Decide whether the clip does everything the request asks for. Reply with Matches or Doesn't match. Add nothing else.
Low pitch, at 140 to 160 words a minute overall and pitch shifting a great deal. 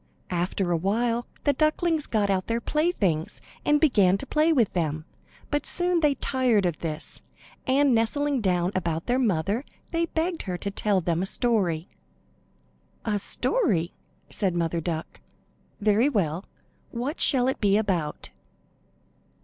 Doesn't match